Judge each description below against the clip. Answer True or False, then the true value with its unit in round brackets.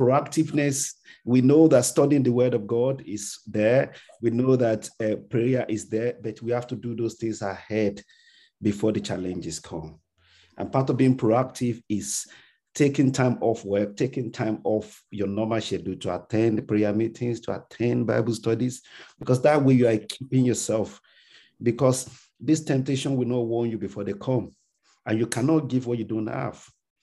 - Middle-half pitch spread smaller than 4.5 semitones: True (3.2 semitones)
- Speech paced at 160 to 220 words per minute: True (175 wpm)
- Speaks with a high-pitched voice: False (115 Hz)